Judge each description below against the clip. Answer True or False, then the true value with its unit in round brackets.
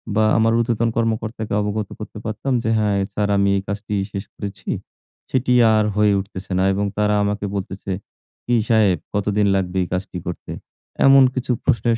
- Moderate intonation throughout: False (2.2 semitones)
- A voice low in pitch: True (105 Hz)